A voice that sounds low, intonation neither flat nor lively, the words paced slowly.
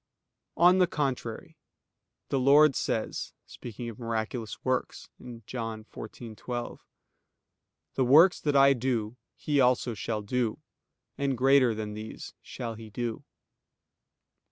Yes: low, 120 Hz; average, 3.5 semitones; slow, 115 wpm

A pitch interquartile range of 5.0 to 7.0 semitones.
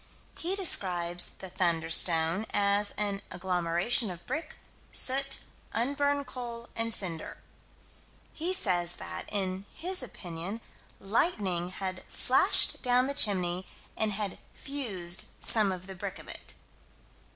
Yes: wide, 5.6 semitones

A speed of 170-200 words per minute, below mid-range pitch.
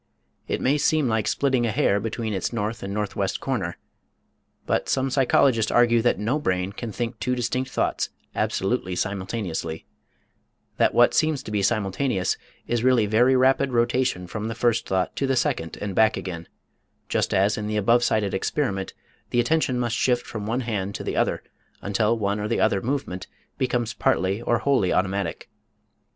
Yes: average, 175 wpm; low, 110 Hz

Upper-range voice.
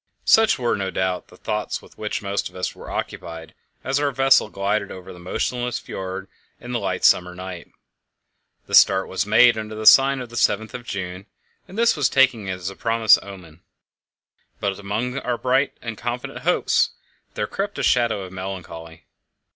No: low, 105 Hz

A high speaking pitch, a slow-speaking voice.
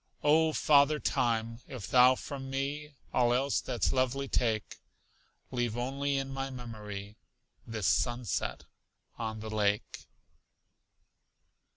No: low, 125 Hz; slow, 110 wpm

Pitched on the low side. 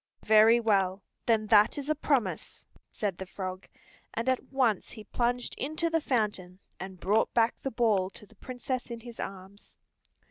No: high, 220 Hz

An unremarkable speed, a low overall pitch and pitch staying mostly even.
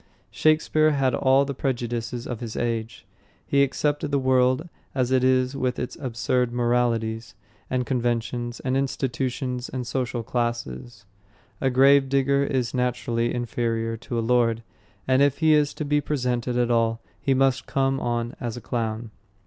Yes: average, 155 wpm; low, 125 Hz; narrow, 2.2 semitones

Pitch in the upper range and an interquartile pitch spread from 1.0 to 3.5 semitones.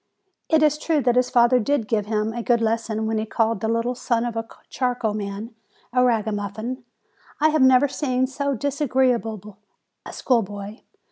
Yes: high, 235 Hz; average, 2.8 semitones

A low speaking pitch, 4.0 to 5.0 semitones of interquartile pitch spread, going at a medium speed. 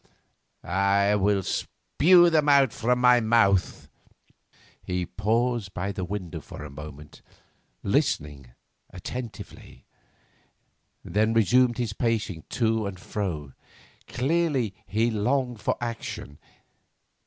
No: low, 105 Hz; average, 4.7 semitones; slow, 100 wpm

